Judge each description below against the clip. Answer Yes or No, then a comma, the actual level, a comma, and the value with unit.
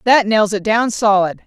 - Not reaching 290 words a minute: Yes, fast, 205 wpm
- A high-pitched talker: Yes, high, 215 Hz